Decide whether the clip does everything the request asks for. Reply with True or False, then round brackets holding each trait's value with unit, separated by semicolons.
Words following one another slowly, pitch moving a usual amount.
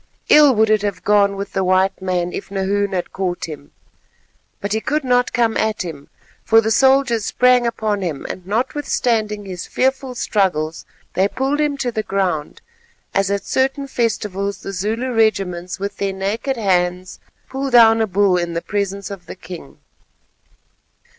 False (165 wpm; 4.0 semitones)